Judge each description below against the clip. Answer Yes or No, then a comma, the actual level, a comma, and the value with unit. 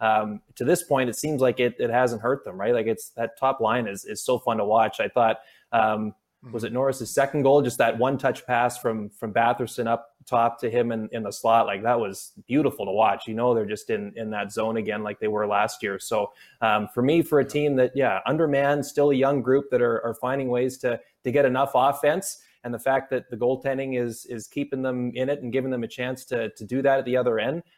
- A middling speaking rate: No, fast, 255 wpm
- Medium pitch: No, low, 125 Hz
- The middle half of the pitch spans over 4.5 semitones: No, average, 2.9 semitones